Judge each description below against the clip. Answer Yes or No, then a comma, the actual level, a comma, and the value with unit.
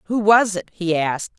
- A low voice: No, high, 190 Hz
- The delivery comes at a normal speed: No, fast, 215 wpm